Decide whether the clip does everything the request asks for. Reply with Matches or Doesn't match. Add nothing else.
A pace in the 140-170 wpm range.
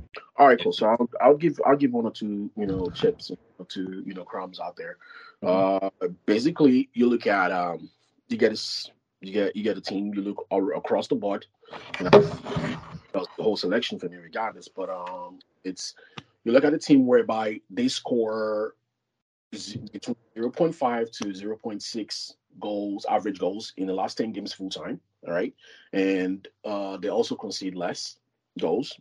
Doesn't match